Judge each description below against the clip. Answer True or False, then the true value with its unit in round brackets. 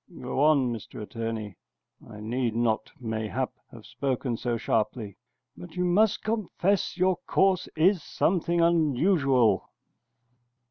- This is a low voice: True (130 Hz)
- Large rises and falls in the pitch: True (7.4 semitones)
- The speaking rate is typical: False (120 wpm)